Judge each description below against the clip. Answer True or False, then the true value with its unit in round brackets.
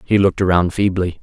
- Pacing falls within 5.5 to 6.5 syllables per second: True (6.3 syllables/s)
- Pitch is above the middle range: False (90 Hz)